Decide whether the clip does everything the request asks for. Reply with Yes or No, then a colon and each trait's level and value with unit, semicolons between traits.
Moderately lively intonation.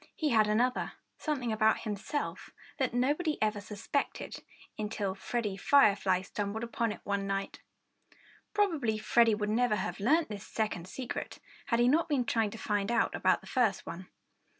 Yes: average, 3.4 semitones